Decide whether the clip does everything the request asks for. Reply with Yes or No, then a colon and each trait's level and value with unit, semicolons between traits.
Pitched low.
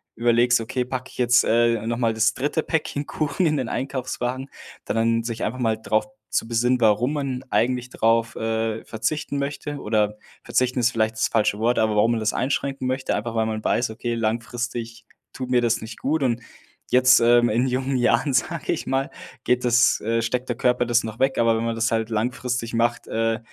Yes: low, 120 Hz